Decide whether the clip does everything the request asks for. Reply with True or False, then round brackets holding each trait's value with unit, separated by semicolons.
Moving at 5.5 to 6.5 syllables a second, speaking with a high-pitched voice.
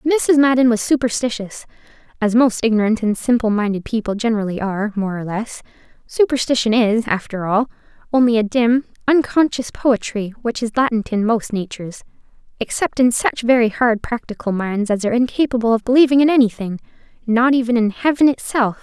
True (5.6 syllables/s; 230 Hz)